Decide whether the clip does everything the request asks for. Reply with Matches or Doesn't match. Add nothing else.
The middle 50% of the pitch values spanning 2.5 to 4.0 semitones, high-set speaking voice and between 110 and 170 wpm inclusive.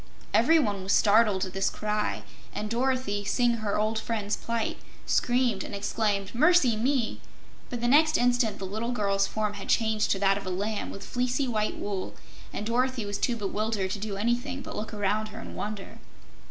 Doesn't match